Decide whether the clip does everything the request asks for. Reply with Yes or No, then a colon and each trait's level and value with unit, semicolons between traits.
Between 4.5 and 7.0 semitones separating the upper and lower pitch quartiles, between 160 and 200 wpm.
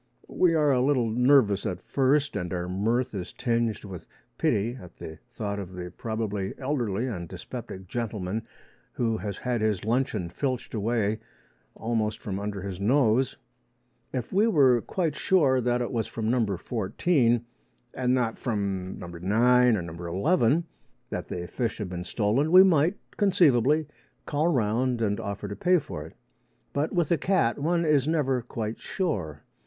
Yes: average, 5.2 semitones; average, 165 wpm